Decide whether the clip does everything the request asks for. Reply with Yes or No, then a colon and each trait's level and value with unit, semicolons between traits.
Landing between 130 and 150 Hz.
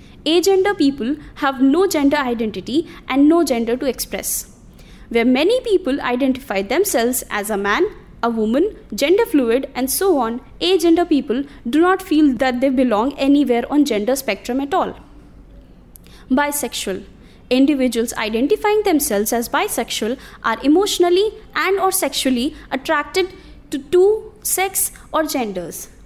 No: very high, 280 Hz